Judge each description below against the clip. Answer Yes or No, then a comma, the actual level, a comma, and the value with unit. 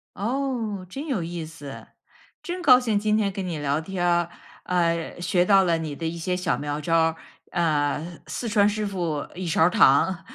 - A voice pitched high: No, medium, 175 Hz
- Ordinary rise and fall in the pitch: Yes, average, 4.0 semitones